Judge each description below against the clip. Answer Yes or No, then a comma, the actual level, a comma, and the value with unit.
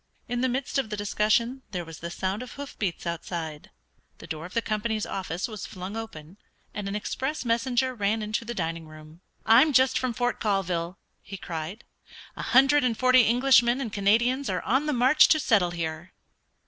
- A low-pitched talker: No, high, 215 Hz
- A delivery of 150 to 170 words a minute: No, average, 190 wpm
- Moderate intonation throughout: No, wide, 5.8 semitones